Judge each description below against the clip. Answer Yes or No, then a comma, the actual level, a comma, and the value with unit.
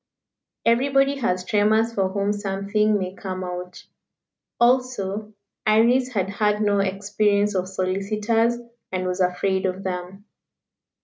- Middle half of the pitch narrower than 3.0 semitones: Yes, narrow, 2.5 semitones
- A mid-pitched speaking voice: No, high, 200 Hz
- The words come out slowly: Yes, slow, 120 wpm